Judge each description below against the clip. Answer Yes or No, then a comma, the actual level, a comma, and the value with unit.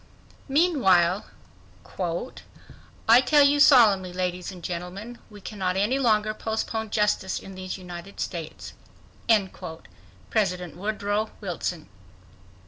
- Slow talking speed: Yes, slow, 90 wpm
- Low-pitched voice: No, high, 200 Hz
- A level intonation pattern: No, average, 3.5 semitones